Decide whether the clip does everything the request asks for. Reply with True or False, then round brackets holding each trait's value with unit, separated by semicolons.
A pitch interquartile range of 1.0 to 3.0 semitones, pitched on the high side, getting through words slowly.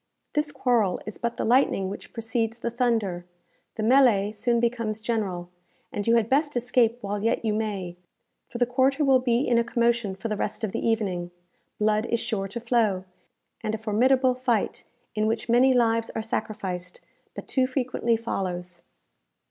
False (2.7 semitones; 230 Hz; 175 wpm)